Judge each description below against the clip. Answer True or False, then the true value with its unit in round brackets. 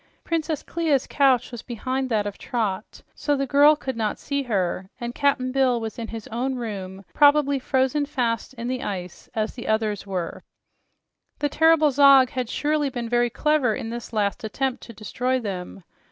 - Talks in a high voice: True (245 Hz)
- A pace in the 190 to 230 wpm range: False (180 wpm)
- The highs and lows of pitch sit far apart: False (4.2 semitones)